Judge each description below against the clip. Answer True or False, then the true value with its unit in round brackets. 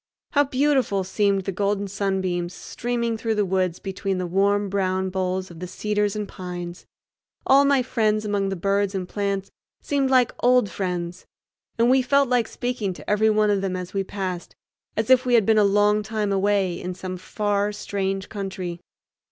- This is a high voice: True (200 Hz)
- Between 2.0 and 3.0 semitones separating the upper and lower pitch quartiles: True (2.5 semitones)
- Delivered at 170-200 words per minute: True (185 wpm)